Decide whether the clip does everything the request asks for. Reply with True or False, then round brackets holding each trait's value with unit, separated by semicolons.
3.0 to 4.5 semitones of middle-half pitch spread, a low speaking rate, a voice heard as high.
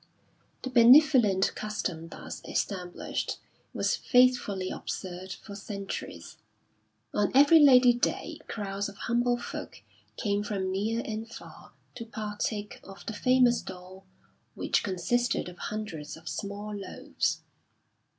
True (3.9 semitones; 120 wpm; 210 Hz)